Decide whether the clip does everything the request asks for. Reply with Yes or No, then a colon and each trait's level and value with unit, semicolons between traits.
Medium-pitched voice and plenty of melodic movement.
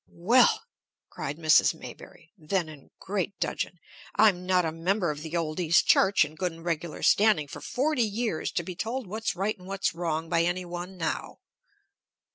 No: medium, 175 Hz; average, 3.4 semitones